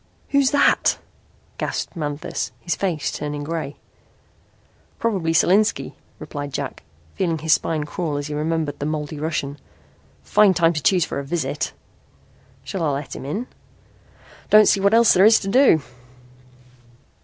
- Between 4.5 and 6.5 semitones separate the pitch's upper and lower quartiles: Yes, average, 4.8 semitones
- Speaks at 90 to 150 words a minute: Yes, average, 145 wpm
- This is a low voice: No, medium, 160 Hz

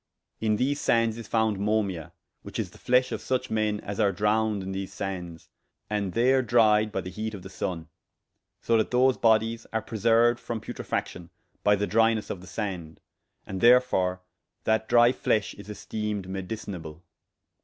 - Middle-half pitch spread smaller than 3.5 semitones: Yes, average, 2.9 semitones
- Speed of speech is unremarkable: Yes, average, 170 wpm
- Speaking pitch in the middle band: No, low, 105 Hz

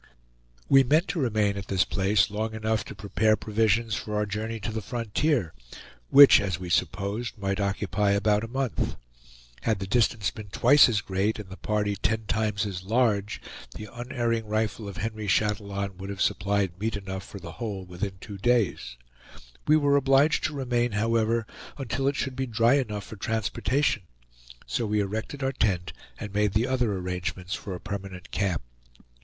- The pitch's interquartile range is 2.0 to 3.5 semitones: Yes, average, 3.0 semitones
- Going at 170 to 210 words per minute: Yes, average, 175 wpm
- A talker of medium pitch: No, low, 105 Hz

